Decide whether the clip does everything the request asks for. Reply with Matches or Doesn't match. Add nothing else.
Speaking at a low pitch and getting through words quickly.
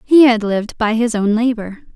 Doesn't match